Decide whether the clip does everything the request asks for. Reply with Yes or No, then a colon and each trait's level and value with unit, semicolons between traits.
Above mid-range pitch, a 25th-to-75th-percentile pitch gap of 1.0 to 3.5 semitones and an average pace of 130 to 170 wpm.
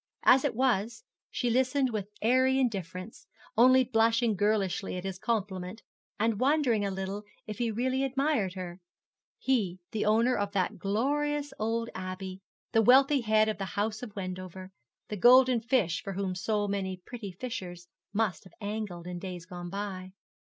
No: high, 210 Hz; average, 4.6 semitones; average, 160 wpm